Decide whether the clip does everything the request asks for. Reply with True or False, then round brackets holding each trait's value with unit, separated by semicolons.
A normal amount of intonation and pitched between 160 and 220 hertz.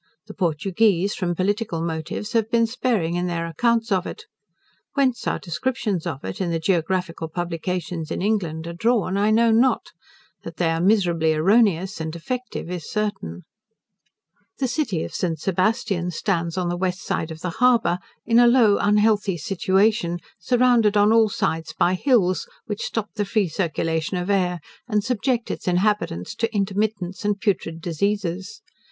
True (4.3 semitones; 190 Hz)